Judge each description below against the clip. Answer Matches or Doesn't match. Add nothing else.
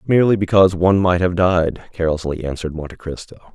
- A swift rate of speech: Doesn't match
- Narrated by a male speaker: Matches